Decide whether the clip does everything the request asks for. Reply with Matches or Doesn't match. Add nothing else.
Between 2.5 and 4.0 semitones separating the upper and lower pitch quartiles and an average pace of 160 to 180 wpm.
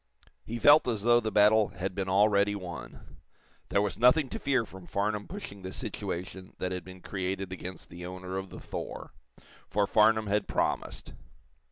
Matches